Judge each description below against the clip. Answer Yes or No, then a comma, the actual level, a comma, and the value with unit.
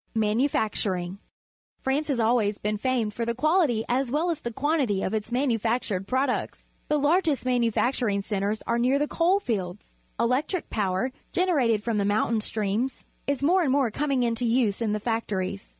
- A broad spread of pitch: No, average, 4.6 semitones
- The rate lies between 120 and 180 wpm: Yes, average, 175 wpm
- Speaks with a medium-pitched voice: No, high, 235 Hz